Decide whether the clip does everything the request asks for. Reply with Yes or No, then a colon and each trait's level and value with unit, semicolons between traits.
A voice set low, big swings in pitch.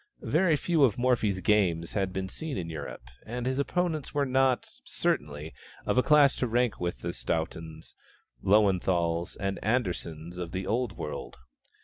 Yes: low, 100 Hz; wide, 7.0 semitones